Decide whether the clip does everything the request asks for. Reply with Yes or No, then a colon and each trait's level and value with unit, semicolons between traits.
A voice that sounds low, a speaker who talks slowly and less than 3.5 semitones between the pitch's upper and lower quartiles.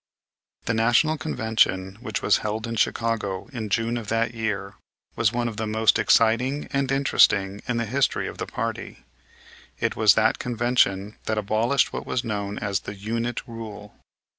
No: low, 110 Hz; average, 165 wpm; narrow, 2.4 semitones